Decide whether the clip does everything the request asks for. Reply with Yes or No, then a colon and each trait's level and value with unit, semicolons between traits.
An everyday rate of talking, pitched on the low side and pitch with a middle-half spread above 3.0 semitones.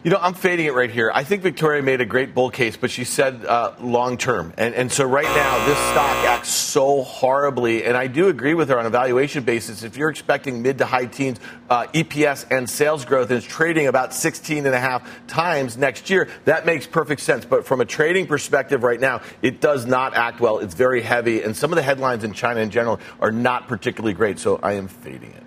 No: fast, 240 wpm; low, 130 Hz; average, 3.5 semitones